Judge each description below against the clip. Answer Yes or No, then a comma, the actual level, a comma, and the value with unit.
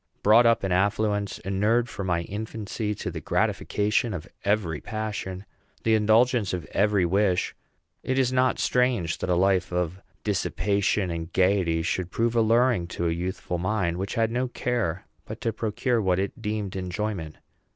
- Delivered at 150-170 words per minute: Yes, average, 160 wpm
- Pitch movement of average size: Yes, average, 3.6 semitones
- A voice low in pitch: Yes, low, 100 Hz